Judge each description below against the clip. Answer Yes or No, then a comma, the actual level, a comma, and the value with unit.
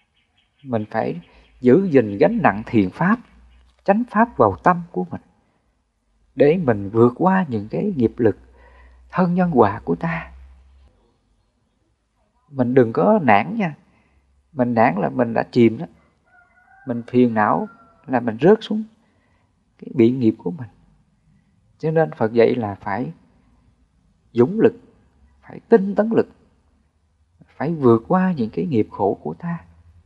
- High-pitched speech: No, low, 115 Hz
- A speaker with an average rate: Yes, average, 145 wpm